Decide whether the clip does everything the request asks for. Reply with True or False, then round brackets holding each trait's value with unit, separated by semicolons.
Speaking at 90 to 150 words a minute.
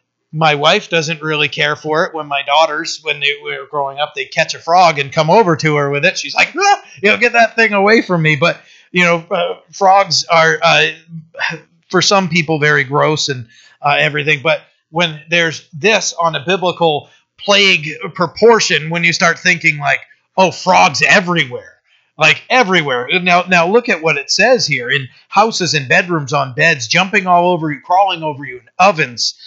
False (190 wpm)